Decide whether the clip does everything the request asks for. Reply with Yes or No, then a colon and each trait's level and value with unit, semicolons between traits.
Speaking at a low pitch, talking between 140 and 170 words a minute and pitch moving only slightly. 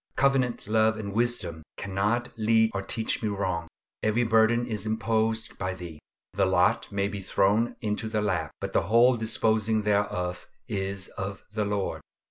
Yes: low, 110 Hz; average, 160 wpm; narrow, 2.3 semitones